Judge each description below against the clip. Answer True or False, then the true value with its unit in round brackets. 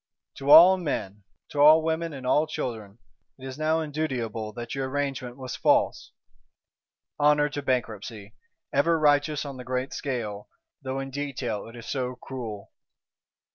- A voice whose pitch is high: False (135 Hz)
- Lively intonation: False (3.7 semitones)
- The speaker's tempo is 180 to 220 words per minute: False (150 wpm)